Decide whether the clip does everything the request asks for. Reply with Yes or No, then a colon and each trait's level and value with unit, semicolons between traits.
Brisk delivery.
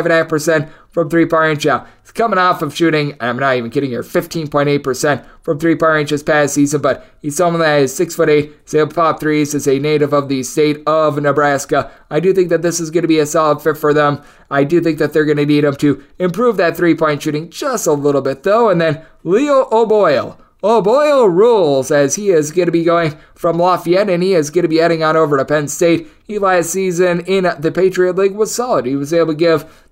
Yes: fast, 240 wpm